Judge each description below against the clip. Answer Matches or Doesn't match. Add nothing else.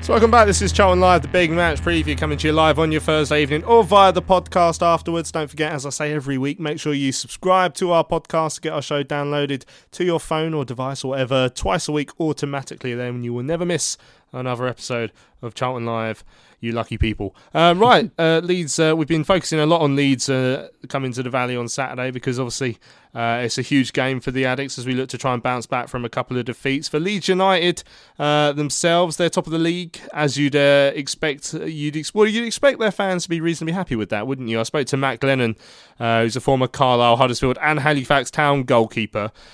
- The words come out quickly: Matches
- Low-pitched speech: Doesn't match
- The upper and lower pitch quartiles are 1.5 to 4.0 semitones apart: Doesn't match